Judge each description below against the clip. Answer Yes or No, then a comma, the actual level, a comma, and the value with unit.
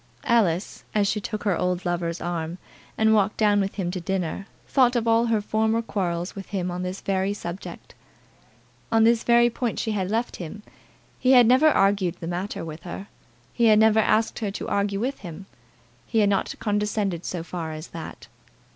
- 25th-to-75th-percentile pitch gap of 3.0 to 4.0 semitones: Yes, average, 3.7 semitones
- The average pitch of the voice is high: Yes, high, 200 Hz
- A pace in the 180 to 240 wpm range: Yes, average, 190 wpm